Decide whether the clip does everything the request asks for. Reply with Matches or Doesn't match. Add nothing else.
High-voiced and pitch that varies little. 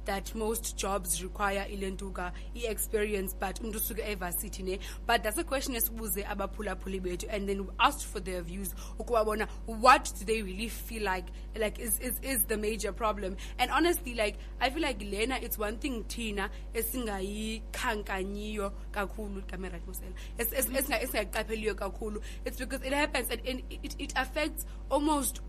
Doesn't match